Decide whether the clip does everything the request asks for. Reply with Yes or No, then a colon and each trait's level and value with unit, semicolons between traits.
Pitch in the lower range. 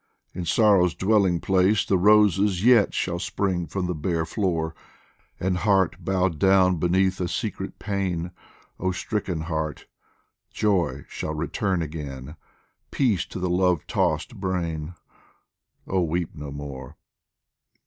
Yes: very low, 90 Hz